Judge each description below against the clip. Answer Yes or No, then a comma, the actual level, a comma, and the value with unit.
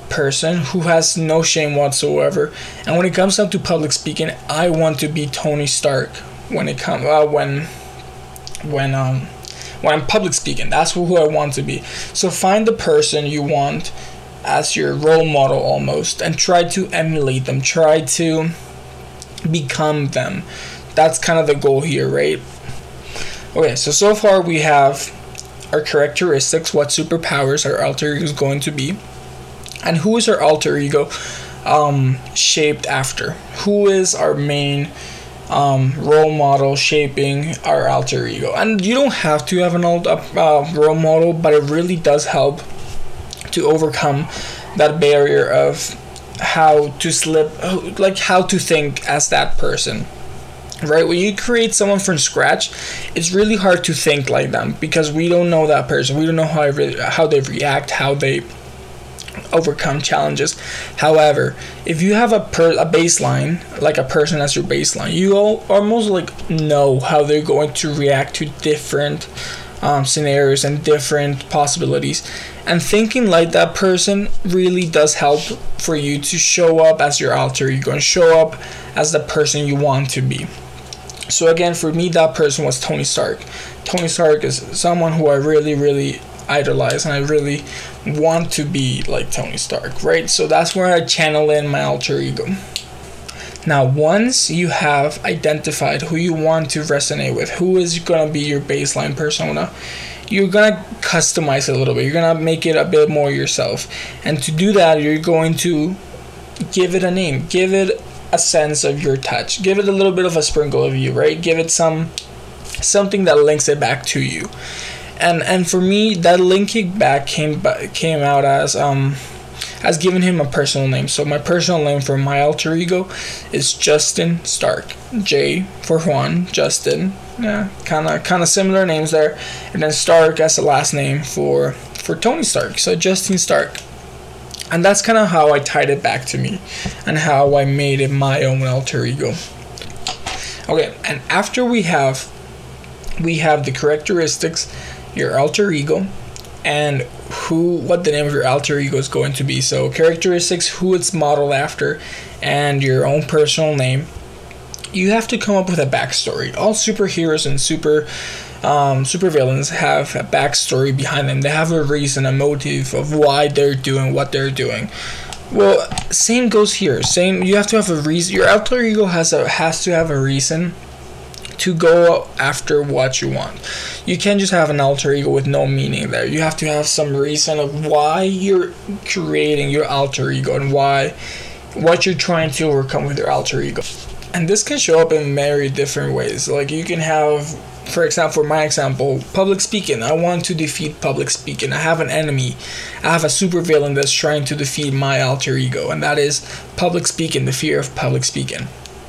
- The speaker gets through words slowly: No, average, 180 wpm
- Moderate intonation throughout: Yes, average, 3.7 semitones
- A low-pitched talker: No, medium, 150 Hz